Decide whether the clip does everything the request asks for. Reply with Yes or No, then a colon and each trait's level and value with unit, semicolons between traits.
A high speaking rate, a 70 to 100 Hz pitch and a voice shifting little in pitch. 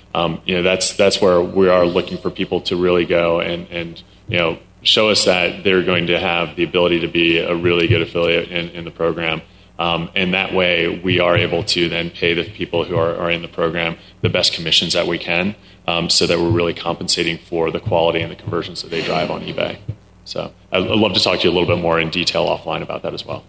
Yes: fast, 245 wpm; very low, 85 Hz; narrow, 1.0 semitones